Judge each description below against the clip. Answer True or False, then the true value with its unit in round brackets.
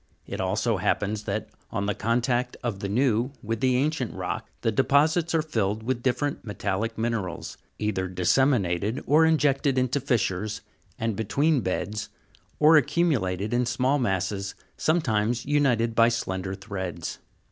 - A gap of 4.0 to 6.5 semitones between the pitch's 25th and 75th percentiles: True (5.0 semitones)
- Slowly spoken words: False (145 wpm)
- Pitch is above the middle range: False (115 Hz)